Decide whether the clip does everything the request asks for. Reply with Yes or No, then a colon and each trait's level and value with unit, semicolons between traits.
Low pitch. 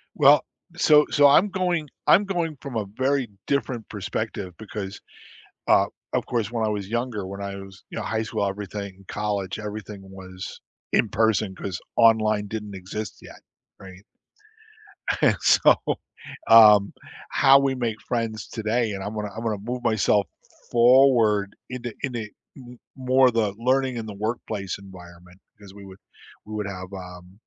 Yes: low, 110 Hz